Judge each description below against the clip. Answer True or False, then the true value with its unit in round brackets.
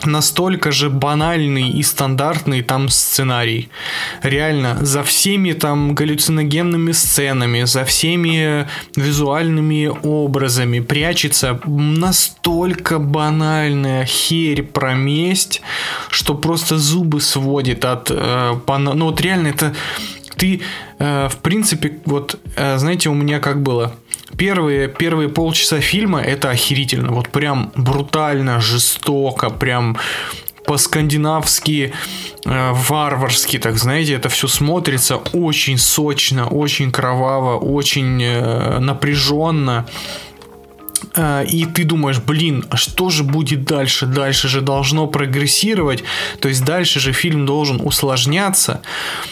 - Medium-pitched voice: True (145 Hz)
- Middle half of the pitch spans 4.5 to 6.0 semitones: False (2.6 semitones)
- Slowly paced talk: True (105 wpm)